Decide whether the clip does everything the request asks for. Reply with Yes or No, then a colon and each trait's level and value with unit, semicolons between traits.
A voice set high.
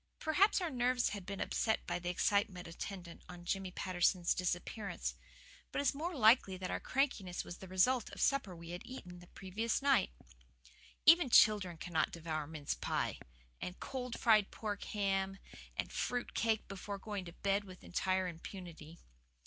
Yes: high, 195 Hz